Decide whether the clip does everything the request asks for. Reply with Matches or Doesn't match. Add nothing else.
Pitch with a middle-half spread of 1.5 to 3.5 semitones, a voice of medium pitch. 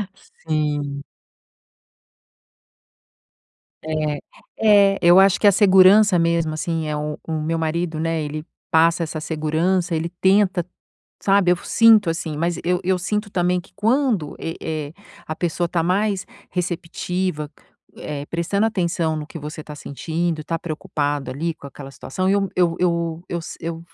Matches